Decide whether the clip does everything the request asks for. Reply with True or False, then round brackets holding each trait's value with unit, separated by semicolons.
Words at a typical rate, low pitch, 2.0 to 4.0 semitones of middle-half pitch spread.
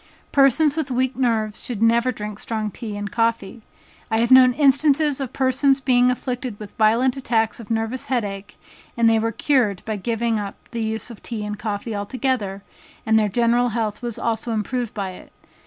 False (185 wpm; 230 Hz; 3.0 semitones)